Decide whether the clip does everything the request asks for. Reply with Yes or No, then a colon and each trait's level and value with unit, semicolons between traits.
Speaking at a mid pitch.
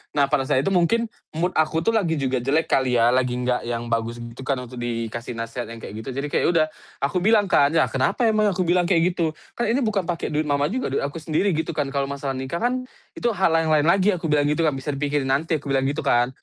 Yes: medium, 150 Hz